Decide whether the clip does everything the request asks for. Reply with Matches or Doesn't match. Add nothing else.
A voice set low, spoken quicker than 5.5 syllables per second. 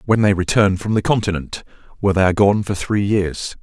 Matches